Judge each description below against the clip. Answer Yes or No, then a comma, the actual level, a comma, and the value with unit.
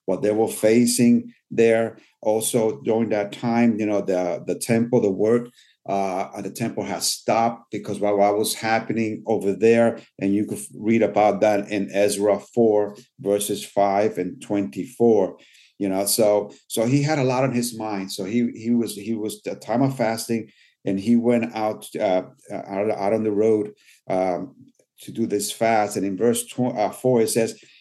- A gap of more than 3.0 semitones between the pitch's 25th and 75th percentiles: No, narrow, 2.4 semitones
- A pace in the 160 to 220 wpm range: Yes, average, 180 wpm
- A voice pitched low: Yes, low, 110 Hz